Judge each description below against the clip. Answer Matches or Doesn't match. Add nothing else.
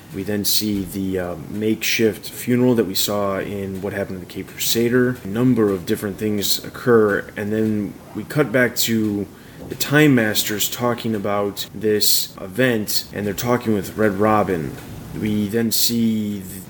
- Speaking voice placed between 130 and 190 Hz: Doesn't match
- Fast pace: Doesn't match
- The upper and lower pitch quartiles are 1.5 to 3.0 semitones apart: Matches